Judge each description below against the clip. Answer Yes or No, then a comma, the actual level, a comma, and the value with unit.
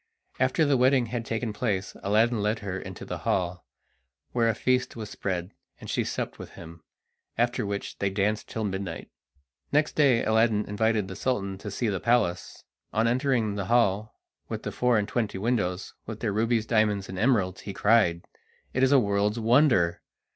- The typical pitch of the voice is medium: No, low, 110 Hz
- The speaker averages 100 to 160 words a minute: No, average, 180 wpm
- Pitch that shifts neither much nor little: Yes, average, 3.4 semitones